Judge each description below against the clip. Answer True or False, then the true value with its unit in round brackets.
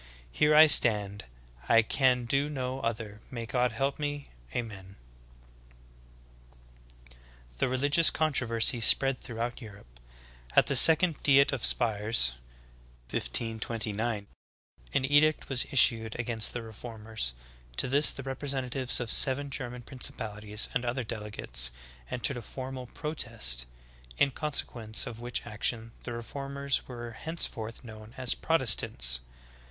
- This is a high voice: False (120 Hz)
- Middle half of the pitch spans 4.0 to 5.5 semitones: False (3.5 semitones)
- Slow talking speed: True (125 wpm)